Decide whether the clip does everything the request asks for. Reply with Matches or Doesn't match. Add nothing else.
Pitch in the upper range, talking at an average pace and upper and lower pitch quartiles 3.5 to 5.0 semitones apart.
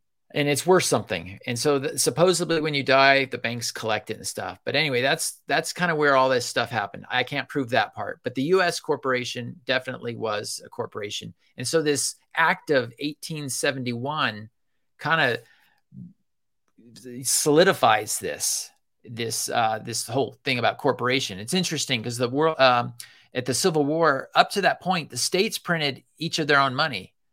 Doesn't match